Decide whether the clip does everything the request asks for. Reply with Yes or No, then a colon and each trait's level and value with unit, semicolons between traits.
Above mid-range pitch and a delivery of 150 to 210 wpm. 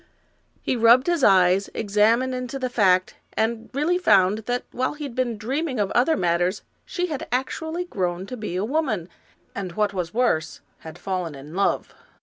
Yes: high, 220 Hz; average, 175 wpm